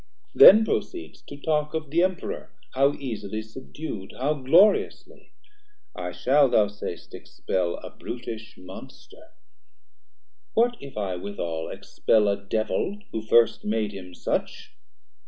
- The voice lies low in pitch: Yes, low, 115 Hz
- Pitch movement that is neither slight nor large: No, wide, 6.8 semitones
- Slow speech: Yes, slow, 125 wpm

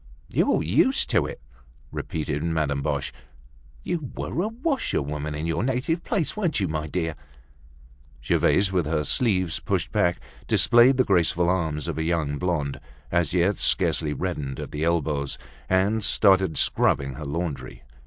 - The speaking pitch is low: Yes, very low, 85 Hz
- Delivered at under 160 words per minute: Yes, average, 150 wpm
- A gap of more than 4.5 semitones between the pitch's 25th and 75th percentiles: Yes, wide, 5.5 semitones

